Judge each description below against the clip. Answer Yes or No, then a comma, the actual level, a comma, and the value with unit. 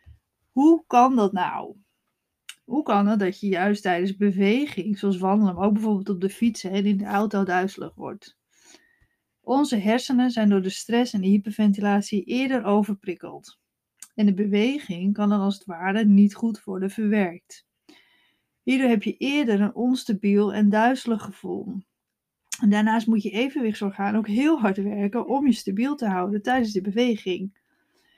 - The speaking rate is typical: Yes, average, 160 wpm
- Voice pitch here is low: No, high, 205 Hz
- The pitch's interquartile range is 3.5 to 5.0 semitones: No, average, 2.9 semitones